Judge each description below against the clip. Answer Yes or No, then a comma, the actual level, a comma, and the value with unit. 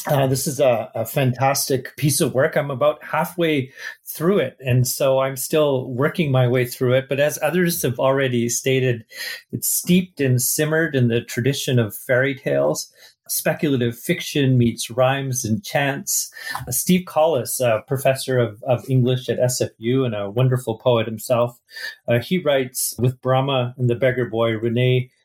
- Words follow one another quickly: No, average, 165 wpm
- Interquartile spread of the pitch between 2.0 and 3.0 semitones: Yes, average, 2.7 semitones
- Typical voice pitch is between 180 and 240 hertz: No, low, 130 Hz